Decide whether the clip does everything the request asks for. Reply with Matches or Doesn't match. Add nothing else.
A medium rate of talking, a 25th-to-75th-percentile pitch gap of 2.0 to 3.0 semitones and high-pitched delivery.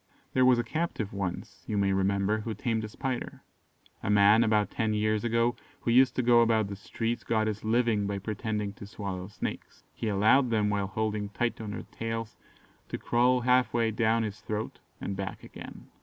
Doesn't match